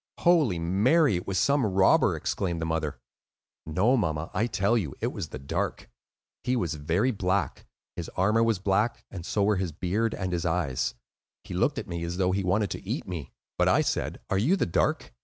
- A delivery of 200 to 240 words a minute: Yes, fast, 205 wpm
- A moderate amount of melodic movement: Yes, average, 4.3 semitones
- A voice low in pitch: Yes, very low, 95 Hz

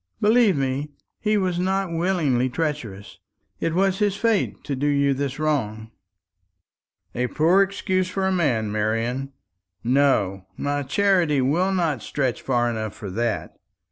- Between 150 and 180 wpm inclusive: No, average, 140 wpm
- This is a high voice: No, medium, 145 Hz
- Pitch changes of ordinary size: No, wide, 7.3 semitones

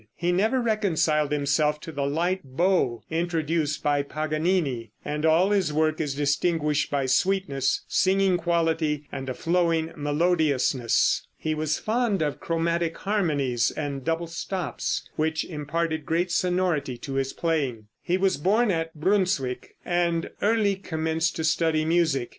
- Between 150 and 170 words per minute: No, average, 140 wpm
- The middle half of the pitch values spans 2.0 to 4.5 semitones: Yes, average, 3.3 semitones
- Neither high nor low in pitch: Yes, medium, 160 Hz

